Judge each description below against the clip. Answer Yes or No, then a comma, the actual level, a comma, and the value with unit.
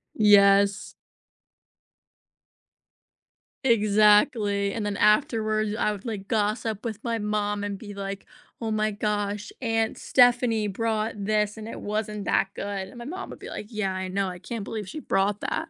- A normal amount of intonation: No, narrow, 1.7 semitones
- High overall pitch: Yes, high, 210 Hz